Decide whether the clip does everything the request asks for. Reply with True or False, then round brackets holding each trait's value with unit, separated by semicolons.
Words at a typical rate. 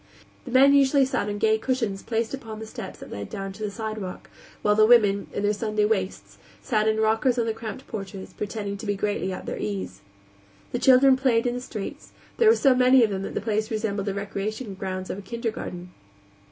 False (220 wpm)